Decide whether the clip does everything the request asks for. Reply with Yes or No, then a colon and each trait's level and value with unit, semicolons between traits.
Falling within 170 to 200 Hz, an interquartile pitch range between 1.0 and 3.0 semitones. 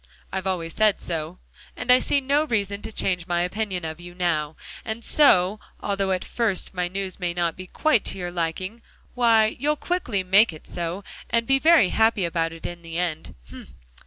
No: high, 190 Hz; average, 4.2 semitones